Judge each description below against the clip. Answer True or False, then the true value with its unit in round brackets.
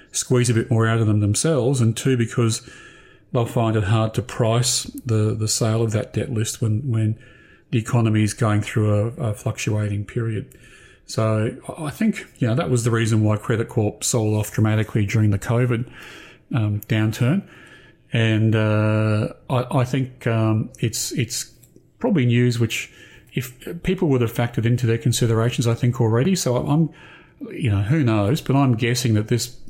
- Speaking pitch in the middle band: False (115 Hz)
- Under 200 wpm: True (180 wpm)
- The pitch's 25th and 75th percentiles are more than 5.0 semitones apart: False (2.4 semitones)